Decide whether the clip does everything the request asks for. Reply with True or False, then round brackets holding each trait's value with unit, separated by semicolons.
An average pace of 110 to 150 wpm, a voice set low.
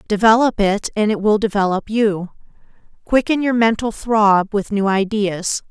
False (145 wpm; 210 Hz)